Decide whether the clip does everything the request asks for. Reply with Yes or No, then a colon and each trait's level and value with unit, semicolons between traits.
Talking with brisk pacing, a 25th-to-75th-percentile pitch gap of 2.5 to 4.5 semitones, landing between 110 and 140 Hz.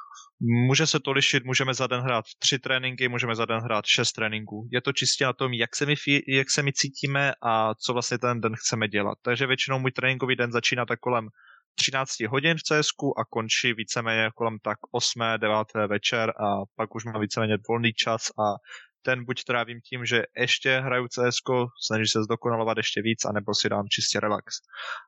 Yes: fast, 195 wpm; average, 2.8 semitones; low, 120 Hz